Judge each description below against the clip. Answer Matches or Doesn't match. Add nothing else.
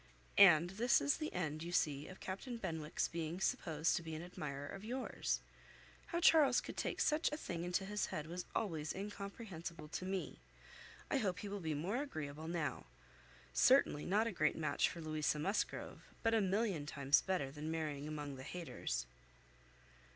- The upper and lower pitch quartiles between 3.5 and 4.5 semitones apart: Doesn't match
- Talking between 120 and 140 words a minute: Doesn't match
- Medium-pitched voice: Matches